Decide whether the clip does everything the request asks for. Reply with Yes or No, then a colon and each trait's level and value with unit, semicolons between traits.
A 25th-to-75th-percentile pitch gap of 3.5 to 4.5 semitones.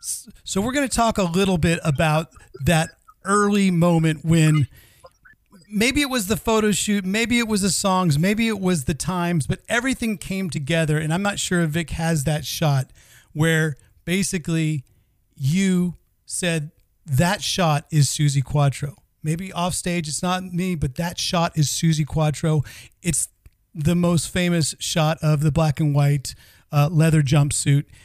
Yes: average, 3.9 semitones